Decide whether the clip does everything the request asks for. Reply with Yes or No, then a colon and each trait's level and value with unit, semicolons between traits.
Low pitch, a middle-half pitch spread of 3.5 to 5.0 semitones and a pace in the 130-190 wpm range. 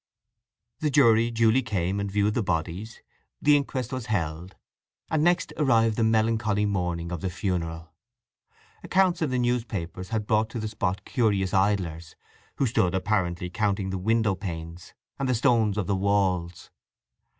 Yes: low, 105 Hz; average, 4.1 semitones; average, 155 wpm